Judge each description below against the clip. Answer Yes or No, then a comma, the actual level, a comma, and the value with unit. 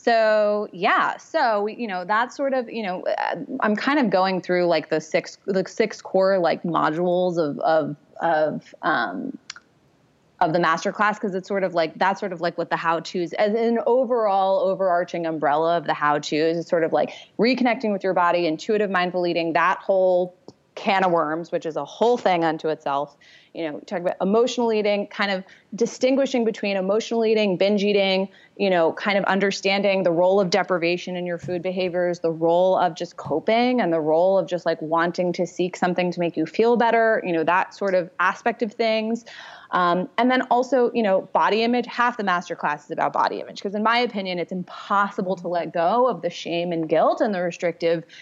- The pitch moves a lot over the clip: No, average, 4.0 semitones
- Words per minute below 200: No, fast, 205 wpm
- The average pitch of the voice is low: No, medium, 185 Hz